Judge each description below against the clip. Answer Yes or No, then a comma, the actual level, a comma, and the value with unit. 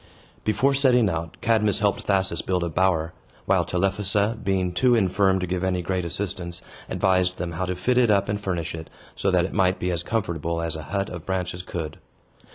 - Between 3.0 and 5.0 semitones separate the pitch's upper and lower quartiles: No, narrow, 2.6 semitones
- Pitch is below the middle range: Yes, very low, 95 Hz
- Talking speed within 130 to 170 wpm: No, average, 200 wpm